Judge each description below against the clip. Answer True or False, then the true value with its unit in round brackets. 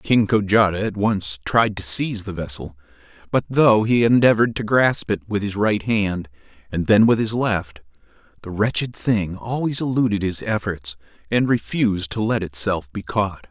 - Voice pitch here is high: False (105 Hz)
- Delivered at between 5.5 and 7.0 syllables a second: False (4.7 syllables/s)